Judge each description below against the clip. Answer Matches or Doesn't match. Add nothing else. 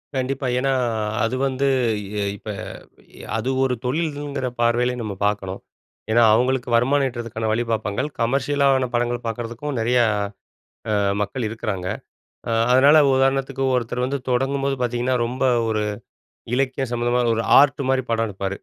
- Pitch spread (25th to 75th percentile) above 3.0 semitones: Doesn't match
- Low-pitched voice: Matches